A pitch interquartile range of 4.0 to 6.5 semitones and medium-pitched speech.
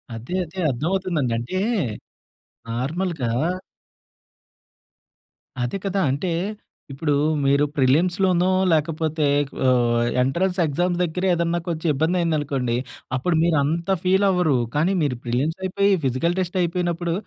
Yes: average, 4.3 semitones; medium, 165 Hz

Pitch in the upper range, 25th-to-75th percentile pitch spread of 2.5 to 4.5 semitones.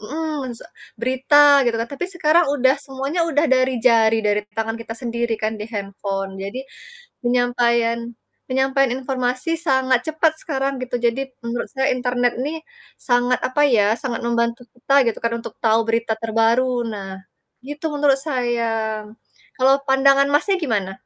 Yes: high, 245 Hz; average, 2.9 semitones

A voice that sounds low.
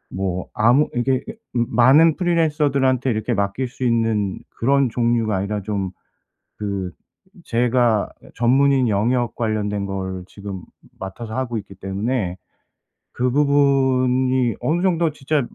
Yes: low, 120 Hz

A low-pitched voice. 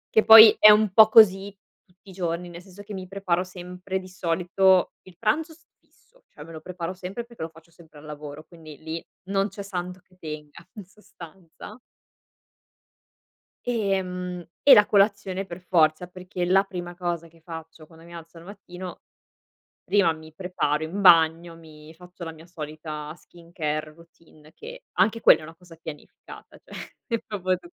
No: medium, 180 Hz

